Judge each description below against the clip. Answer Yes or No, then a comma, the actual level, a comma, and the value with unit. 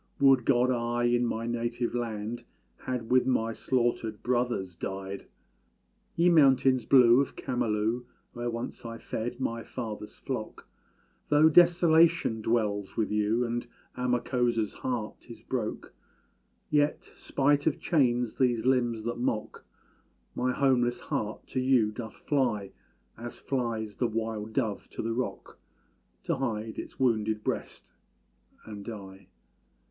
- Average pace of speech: No, slow, 130 wpm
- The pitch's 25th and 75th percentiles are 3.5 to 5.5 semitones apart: No, narrow, 2.5 semitones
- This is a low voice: Yes, low, 120 Hz